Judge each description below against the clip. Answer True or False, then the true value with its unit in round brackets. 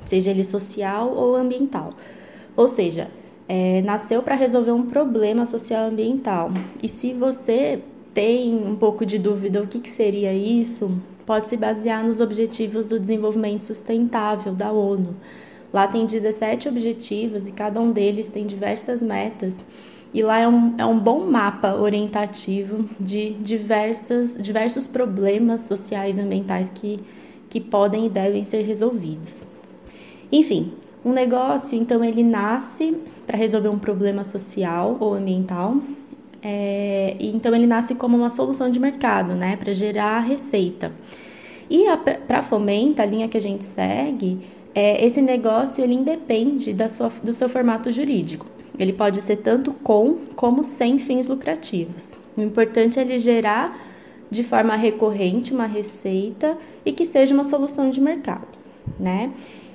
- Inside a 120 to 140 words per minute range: False (150 wpm)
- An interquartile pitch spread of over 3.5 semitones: False (3.2 semitones)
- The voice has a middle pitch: False (225 Hz)